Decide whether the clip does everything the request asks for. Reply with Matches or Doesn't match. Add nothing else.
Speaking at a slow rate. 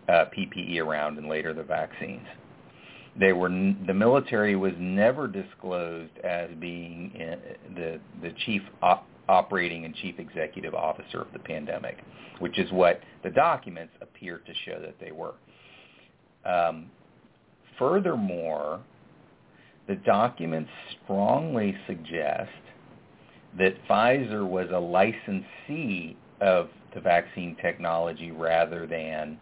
Matches